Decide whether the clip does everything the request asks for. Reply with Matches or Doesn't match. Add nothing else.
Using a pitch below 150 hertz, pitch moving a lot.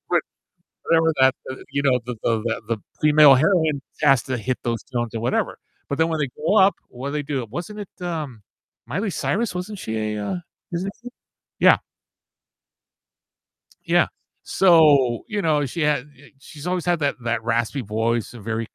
Matches